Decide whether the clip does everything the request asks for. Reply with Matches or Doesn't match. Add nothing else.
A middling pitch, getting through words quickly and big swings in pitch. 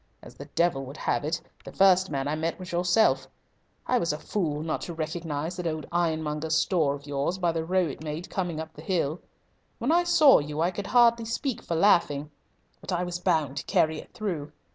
Doesn't match